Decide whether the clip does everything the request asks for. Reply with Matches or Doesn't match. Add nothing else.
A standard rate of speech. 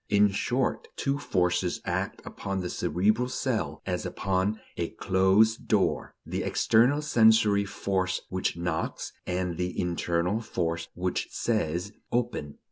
Doesn't match